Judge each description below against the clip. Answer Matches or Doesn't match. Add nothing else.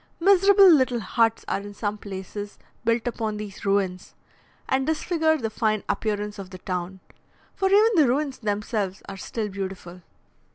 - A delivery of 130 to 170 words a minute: Matches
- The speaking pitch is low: Doesn't match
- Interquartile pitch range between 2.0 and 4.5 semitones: Doesn't match